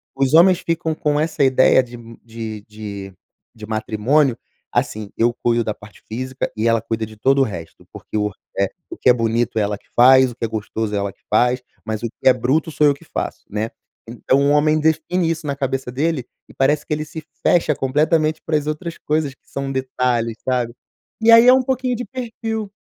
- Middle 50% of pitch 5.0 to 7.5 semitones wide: Yes, average, 5.3 semitones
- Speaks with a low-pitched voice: Yes, low, 130 Hz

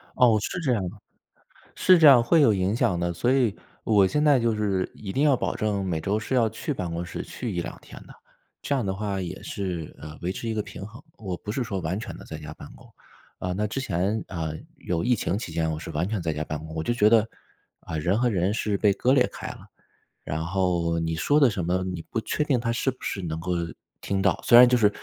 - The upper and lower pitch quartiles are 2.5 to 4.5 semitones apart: No, average, 5.2 semitones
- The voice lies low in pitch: Yes, low, 100 Hz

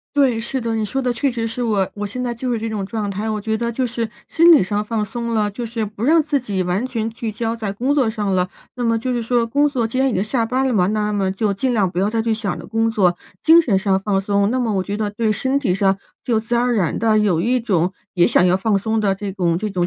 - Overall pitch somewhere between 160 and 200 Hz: No, high, 220 Hz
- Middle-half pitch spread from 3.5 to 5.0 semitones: No, average, 3.1 semitones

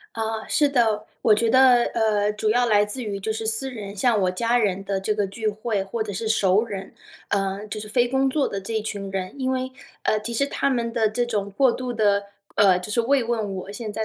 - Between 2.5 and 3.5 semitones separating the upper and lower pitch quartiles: Yes, average, 2.8 semitones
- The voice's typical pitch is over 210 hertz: Yes, high, 220 Hz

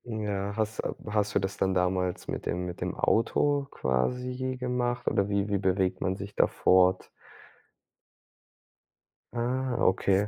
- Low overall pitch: Yes, low, 100 Hz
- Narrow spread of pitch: No, average, 4.5 semitones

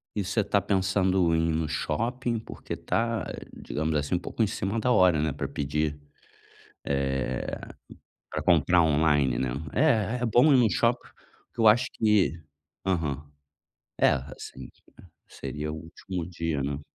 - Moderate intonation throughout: No, wide, 6.3 semitones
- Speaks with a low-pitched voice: Yes, very low, 85 Hz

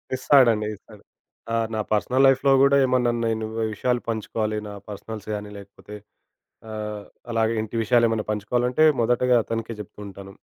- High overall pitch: No, low, 110 Hz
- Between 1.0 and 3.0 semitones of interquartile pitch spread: Yes, narrow, 2.6 semitones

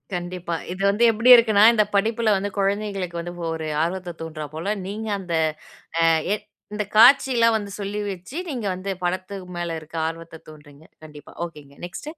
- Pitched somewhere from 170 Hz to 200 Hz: Yes, medium, 185 Hz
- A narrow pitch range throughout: No, average, 4.1 semitones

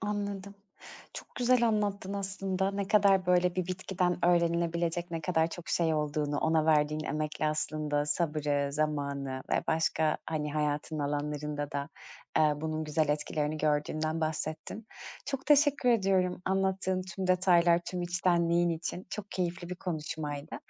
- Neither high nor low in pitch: Yes, medium, 170 Hz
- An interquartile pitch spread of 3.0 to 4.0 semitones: Yes, average, 3.6 semitones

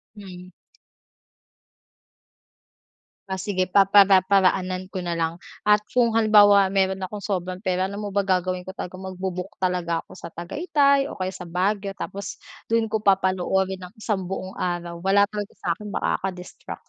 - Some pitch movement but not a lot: No, narrow, 1.9 semitones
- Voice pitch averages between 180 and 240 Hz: Yes, high, 190 Hz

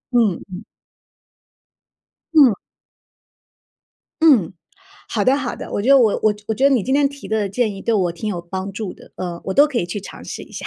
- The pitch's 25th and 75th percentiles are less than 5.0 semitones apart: No, average, 5.3 semitones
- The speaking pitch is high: Yes, high, 215 Hz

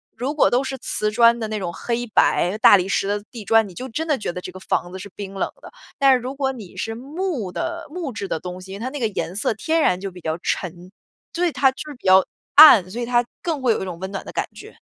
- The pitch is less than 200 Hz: No, high, 225 Hz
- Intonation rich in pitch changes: Yes, wide, 5.9 semitones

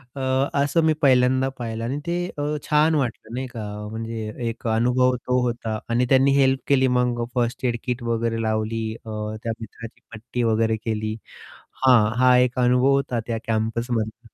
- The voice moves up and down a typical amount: No, narrow, 2.2 semitones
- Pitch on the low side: Yes, low, 120 Hz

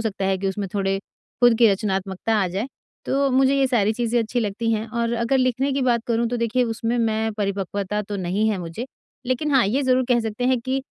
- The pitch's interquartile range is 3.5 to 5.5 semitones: Yes, average, 3.8 semitones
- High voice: Yes, high, 230 Hz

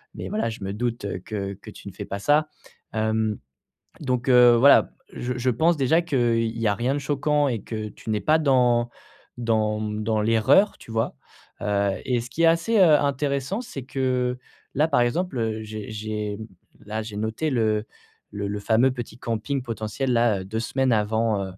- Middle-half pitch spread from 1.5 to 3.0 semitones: No, average, 3.8 semitones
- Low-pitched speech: Yes, low, 115 Hz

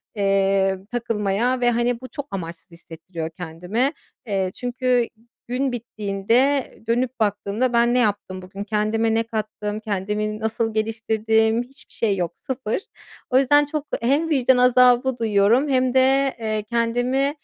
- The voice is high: Yes, high, 230 Hz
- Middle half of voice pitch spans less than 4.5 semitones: Yes, average, 3.5 semitones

